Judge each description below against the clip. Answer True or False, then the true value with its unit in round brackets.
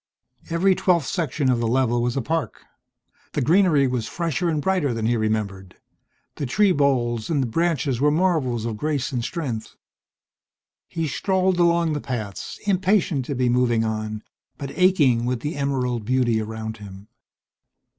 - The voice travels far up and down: True (6.0 semitones)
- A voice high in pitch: False (130 Hz)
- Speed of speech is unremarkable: True (160 wpm)